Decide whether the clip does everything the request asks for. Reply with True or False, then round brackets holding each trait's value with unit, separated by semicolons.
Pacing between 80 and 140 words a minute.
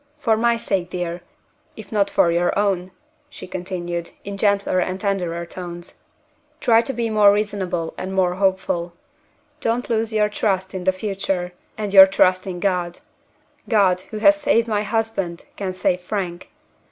False (160 wpm)